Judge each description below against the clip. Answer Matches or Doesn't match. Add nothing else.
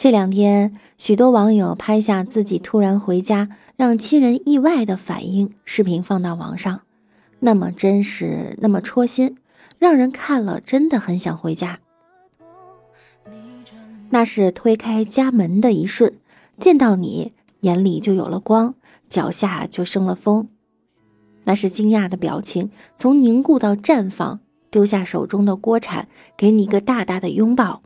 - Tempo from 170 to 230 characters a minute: Matches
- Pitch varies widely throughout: Doesn't match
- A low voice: Doesn't match